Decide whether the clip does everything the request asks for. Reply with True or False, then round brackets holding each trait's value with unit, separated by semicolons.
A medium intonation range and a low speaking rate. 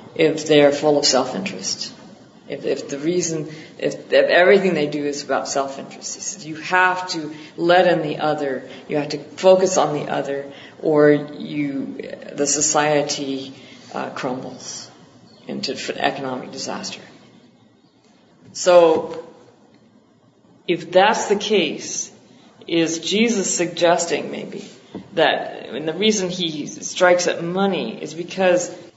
True (3.5 semitones; 130 wpm)